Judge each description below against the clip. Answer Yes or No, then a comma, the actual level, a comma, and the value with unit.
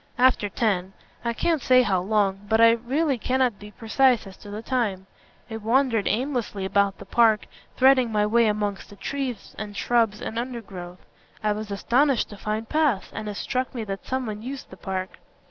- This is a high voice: Yes, high, 220 Hz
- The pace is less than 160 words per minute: No, average, 185 wpm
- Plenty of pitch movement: No, average, 3.6 semitones